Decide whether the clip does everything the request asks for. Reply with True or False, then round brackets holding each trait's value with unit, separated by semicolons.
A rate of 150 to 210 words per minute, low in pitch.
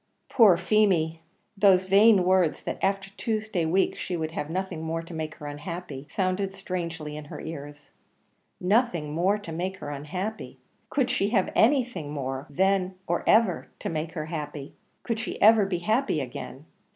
False (165 wpm; 180 Hz)